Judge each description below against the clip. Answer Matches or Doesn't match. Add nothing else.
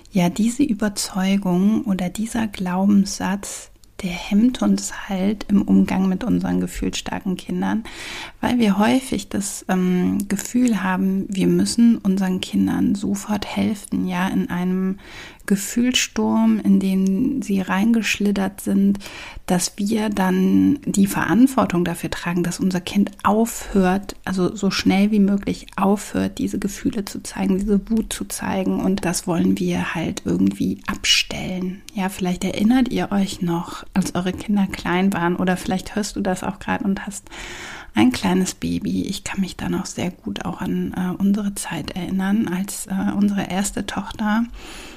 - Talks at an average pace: Matches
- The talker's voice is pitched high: Matches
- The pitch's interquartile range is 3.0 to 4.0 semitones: Doesn't match